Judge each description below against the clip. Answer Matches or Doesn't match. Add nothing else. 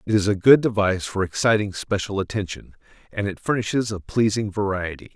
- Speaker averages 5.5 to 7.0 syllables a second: Matches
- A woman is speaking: Doesn't match